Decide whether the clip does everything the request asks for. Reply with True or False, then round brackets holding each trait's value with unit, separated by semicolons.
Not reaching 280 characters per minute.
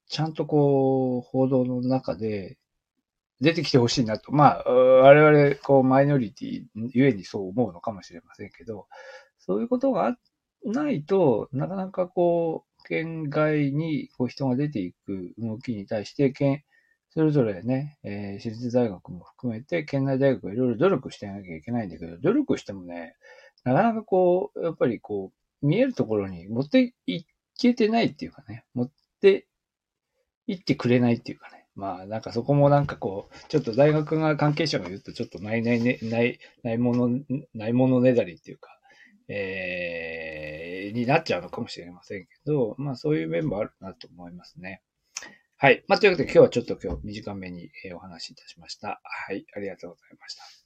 False (365 characters per minute)